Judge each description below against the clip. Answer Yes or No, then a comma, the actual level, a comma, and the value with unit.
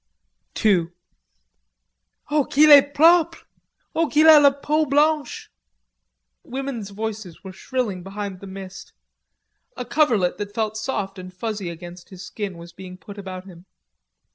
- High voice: Yes, high, 210 Hz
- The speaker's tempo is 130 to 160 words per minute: Yes, average, 140 wpm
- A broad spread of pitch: Yes, wide, 7.1 semitones